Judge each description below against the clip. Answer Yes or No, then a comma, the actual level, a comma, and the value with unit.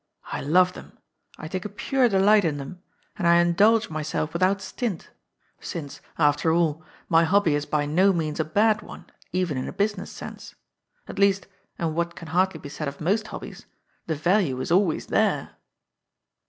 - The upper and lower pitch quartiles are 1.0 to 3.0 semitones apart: No, average, 4.2 semitones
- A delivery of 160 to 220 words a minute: Yes, average, 180 wpm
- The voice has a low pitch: No, medium, 170 Hz